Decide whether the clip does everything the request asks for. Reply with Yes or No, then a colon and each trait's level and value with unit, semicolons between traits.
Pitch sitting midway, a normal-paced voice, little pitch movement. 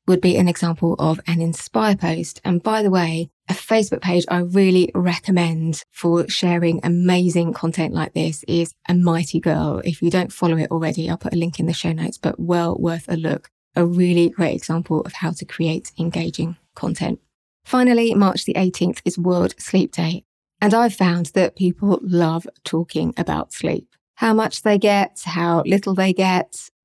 Yes: medium, 175 Hz; average, 185 wpm; narrow, 1.9 semitones